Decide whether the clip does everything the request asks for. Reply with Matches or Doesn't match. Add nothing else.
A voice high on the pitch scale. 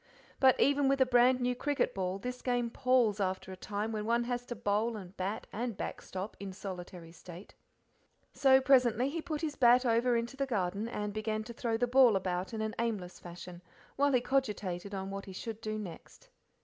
Matches